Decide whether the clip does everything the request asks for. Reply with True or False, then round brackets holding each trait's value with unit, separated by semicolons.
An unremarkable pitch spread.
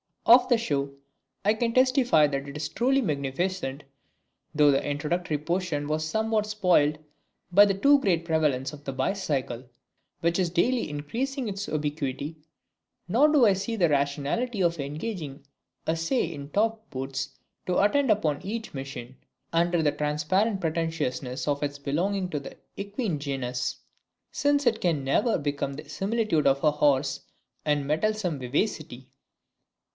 False (6.6 semitones)